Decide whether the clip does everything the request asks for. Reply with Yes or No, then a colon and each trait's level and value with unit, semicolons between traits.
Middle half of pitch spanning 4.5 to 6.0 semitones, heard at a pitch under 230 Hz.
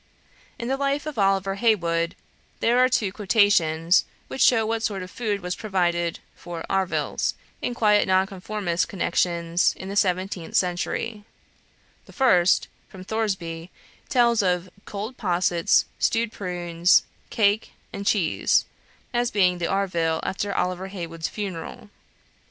No: average, 3.5 semitones; high, 190 Hz